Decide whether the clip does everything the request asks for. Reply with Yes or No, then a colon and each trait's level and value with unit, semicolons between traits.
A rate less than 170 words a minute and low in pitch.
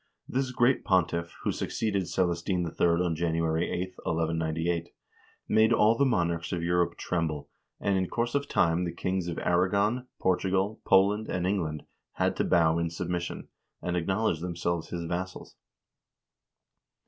Yes: average, 150 wpm; very low, 90 Hz